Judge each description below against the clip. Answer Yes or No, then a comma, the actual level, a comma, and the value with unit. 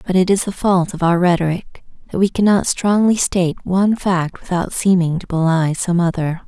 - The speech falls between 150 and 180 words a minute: No, average, 195 wpm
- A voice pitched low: No, medium, 180 Hz